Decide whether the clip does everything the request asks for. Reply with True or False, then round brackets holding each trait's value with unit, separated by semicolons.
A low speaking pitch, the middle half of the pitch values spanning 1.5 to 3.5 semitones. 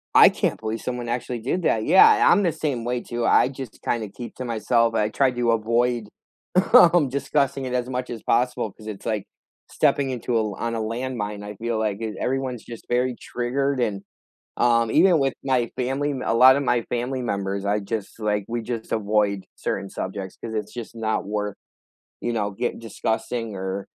True (115 Hz; 2.8 semitones)